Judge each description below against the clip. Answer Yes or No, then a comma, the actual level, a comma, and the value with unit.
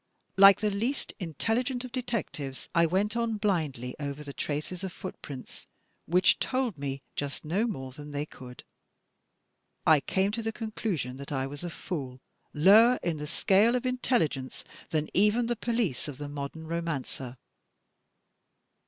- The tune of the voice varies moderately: No, wide, 7.5 semitones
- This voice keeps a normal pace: Yes, average, 155 wpm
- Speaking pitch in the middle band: Yes, medium, 170 Hz